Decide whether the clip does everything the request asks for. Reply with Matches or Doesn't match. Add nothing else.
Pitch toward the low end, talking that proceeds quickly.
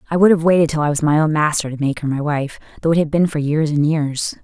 Doesn't match